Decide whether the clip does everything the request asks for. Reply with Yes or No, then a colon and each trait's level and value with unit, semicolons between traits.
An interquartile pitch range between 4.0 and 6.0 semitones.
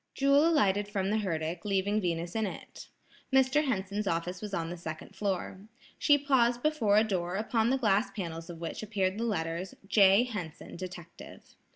Yes: average, 4.3 semitones